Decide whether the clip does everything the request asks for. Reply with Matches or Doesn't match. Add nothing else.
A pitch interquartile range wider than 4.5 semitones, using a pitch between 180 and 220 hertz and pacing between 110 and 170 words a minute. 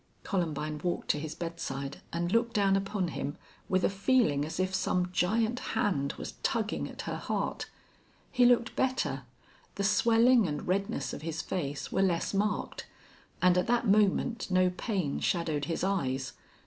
Matches